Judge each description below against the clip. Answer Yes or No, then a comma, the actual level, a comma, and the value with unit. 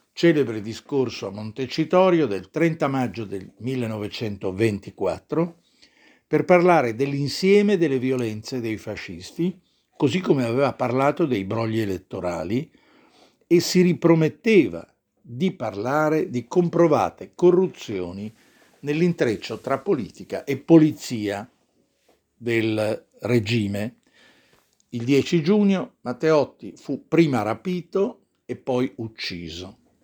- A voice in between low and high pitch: No, low, 130 Hz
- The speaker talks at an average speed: No, slow, 95 wpm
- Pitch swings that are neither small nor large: No, wide, 7.0 semitones